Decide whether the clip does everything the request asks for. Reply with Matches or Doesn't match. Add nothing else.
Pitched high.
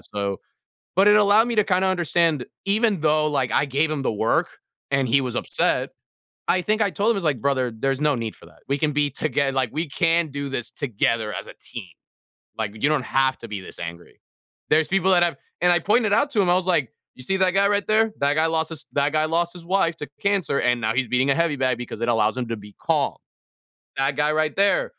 Doesn't match